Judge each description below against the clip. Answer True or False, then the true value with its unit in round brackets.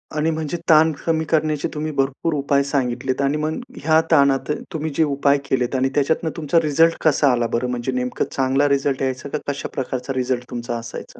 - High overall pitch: False (140 Hz)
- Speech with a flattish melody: False (3.1 semitones)